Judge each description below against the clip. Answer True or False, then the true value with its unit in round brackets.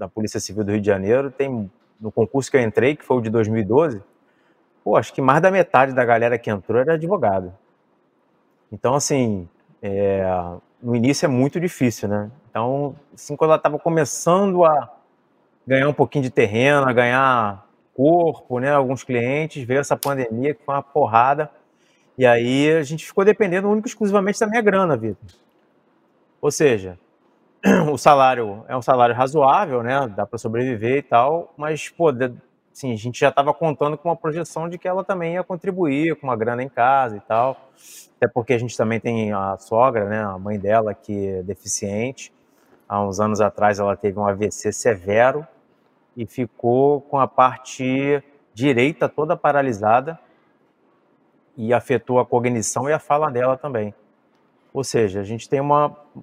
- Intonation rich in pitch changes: False (4.9 semitones)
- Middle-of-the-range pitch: False (130 Hz)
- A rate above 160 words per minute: True (170 wpm)